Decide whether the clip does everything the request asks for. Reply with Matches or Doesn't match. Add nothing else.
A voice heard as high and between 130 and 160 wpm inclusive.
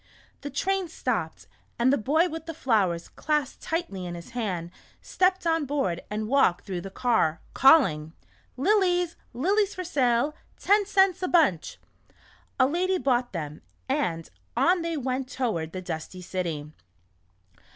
Matches